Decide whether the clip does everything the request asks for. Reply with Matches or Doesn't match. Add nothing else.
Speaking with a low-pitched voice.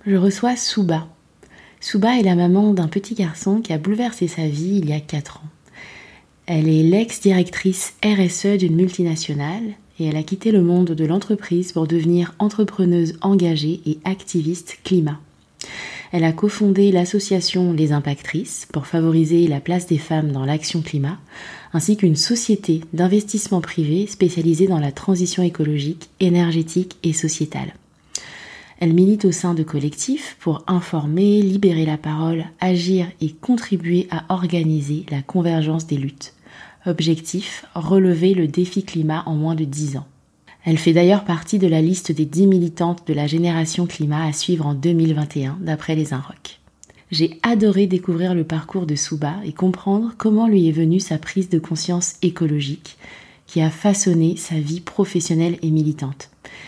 Doesn't match